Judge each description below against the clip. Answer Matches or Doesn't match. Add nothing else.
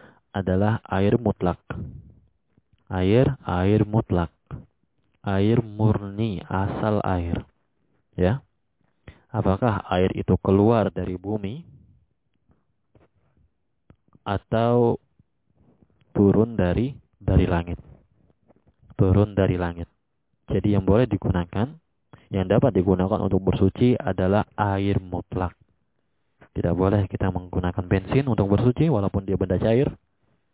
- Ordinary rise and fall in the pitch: Matches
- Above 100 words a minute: Doesn't match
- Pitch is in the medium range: Doesn't match